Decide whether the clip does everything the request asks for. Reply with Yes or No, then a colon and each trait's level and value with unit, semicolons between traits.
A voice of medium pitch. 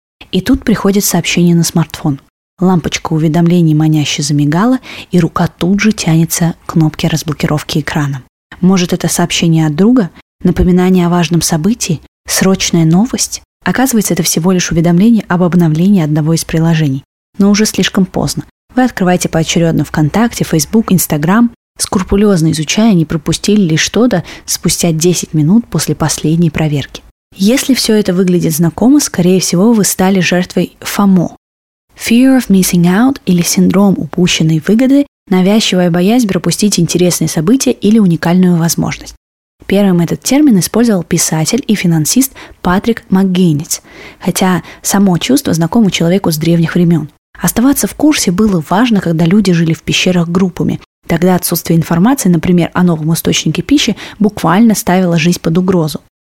Yes: medium, 180 Hz